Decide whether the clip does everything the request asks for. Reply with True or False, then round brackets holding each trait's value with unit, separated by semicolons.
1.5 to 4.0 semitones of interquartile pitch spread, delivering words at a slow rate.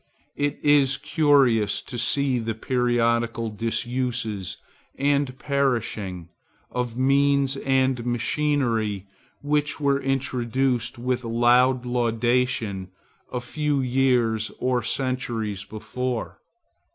True (2.8 semitones; 90 wpm)